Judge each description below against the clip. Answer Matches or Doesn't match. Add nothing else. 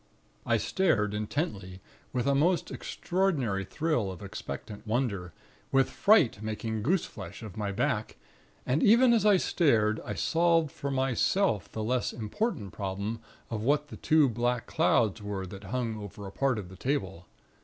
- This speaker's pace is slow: Doesn't match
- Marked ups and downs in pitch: Matches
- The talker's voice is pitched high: Doesn't match